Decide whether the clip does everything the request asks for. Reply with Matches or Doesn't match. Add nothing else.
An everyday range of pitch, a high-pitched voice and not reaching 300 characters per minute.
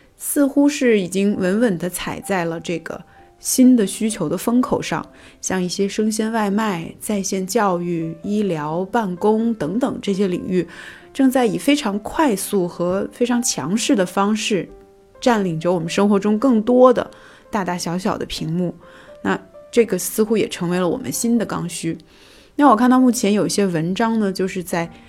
Matches